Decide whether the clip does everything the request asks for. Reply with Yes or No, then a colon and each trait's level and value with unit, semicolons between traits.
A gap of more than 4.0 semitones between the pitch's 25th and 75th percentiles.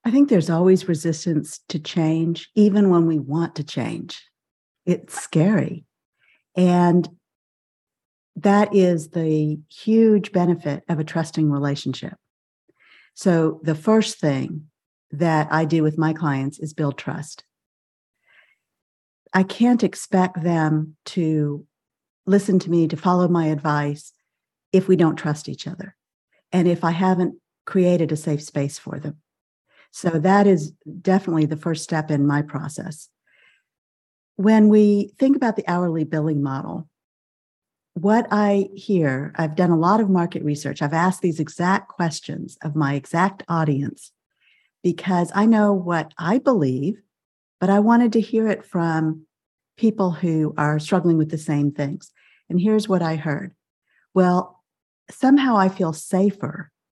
No: average, 3.6 semitones